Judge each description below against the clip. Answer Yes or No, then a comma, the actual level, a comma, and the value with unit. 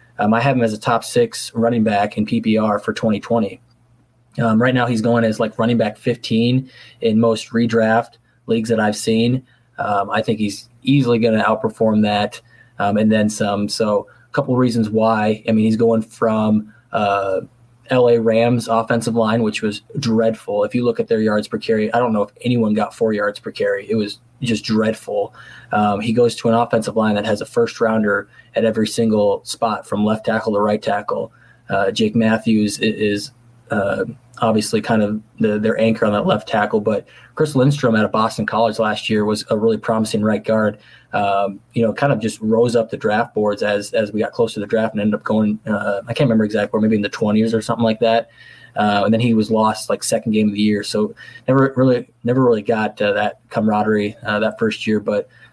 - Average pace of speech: No, fast, 215 wpm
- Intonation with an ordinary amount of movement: No, narrow, 1.6 semitones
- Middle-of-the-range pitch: No, low, 110 Hz